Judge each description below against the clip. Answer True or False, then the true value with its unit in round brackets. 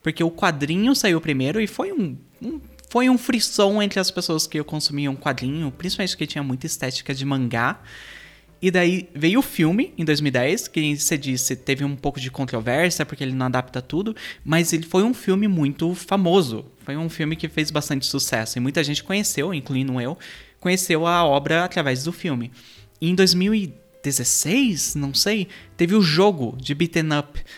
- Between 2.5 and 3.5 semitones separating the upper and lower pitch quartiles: False (5.1 semitones)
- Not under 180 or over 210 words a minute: True (185 wpm)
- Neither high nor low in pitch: True (160 Hz)